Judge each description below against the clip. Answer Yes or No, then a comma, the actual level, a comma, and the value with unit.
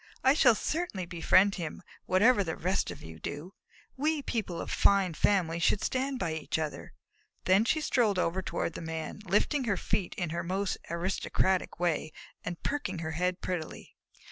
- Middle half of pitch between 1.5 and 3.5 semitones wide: No, average, 3.9 semitones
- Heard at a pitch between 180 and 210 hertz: Yes, medium, 185 Hz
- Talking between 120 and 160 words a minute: No, average, 170 wpm